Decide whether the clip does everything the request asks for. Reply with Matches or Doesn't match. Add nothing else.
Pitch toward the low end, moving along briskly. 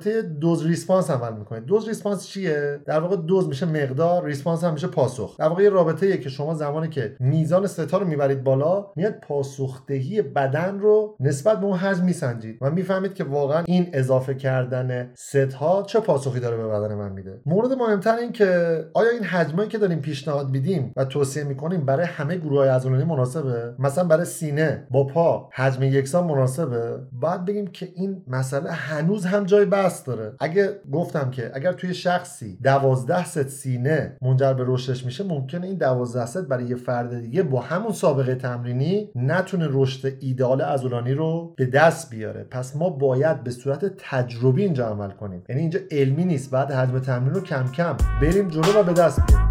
Doesn't match